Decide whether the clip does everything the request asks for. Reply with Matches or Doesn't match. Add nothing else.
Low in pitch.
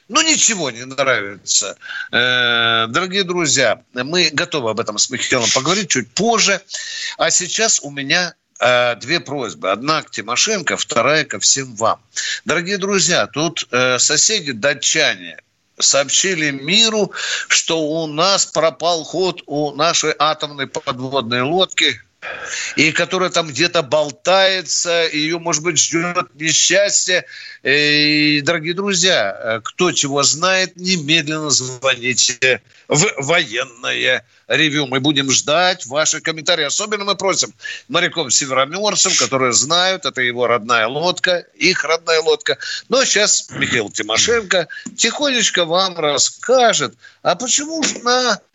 Doesn't match